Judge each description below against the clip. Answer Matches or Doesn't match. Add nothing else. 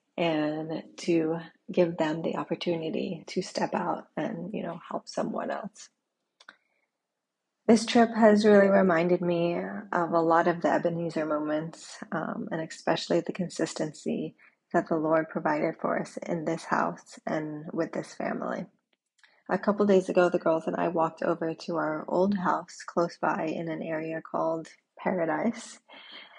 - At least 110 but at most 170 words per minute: Matches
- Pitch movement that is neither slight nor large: Doesn't match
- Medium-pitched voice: Matches